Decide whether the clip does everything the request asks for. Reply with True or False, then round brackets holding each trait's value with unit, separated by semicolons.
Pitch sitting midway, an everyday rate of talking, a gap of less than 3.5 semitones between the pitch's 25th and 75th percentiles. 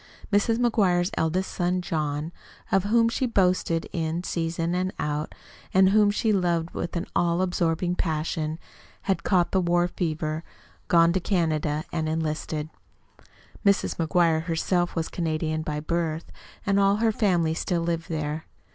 True (170 Hz; 150 wpm; 2.7 semitones)